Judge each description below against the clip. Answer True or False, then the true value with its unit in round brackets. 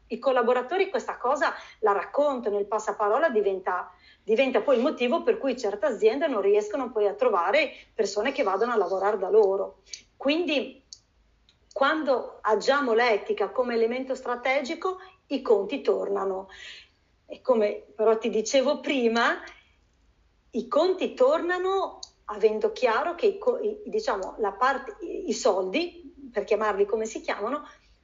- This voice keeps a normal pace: True (135 wpm)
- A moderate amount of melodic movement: False (8.2 semitones)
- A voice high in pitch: True (260 Hz)